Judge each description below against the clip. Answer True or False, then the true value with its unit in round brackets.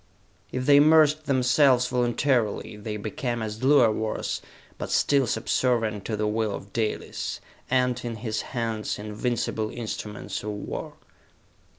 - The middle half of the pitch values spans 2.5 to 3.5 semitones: True (3.0 semitones)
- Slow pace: True (130 wpm)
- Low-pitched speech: True (115 Hz)